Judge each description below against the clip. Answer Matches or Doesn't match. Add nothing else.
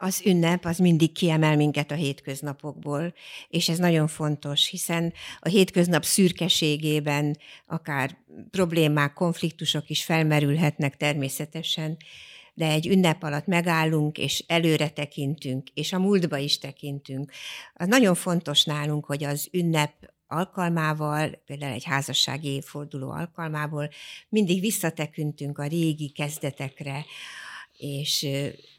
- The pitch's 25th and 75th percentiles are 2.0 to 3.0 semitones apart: Matches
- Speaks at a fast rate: Doesn't match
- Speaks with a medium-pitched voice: Matches